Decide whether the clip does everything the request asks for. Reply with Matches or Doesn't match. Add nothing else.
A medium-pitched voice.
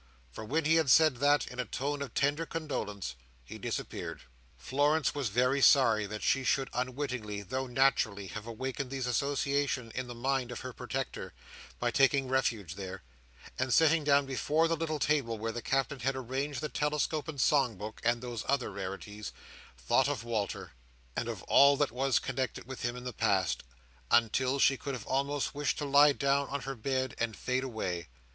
Doesn't match